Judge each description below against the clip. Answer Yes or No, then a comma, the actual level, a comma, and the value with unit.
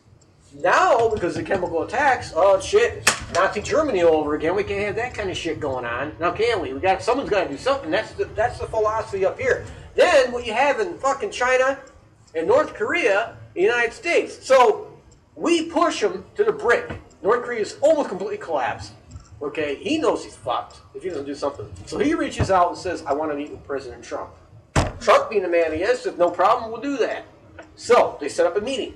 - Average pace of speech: No, fast, 220 wpm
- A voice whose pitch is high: Yes, very high, 255 Hz